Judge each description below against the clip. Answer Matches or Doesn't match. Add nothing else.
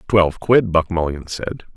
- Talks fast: Doesn't match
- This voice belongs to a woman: Doesn't match